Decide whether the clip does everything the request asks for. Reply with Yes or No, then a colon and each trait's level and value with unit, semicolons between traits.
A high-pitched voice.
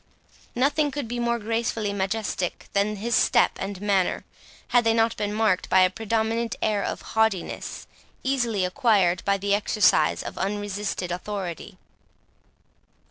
Yes: high, 210 Hz